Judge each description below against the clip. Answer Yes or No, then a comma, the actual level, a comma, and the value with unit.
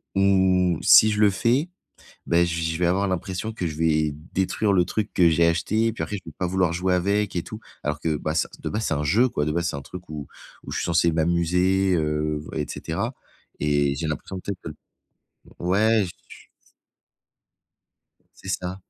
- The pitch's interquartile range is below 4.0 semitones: Yes, average, 3.4 semitones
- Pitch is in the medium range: No, very low, 90 Hz